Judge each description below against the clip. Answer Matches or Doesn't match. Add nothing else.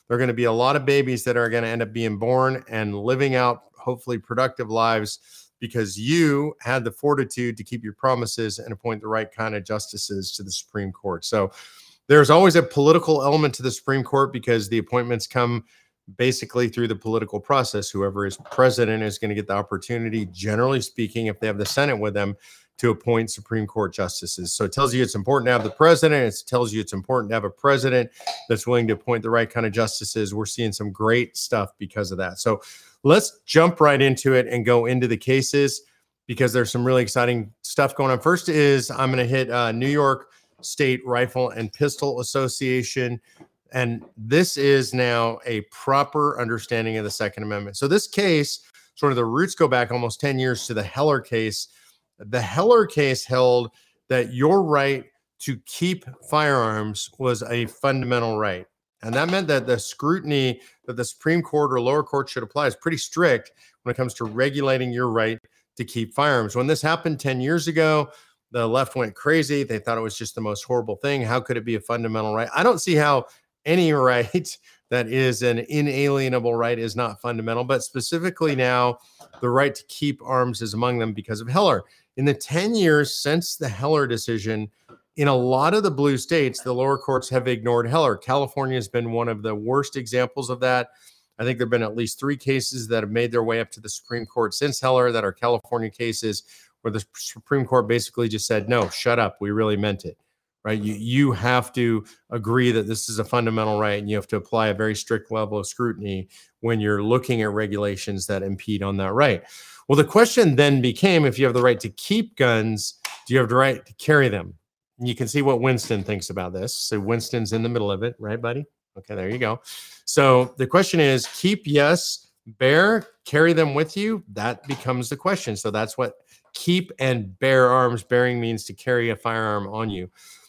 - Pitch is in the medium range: Doesn't match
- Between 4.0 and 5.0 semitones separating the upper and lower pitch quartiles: Doesn't match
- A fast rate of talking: Matches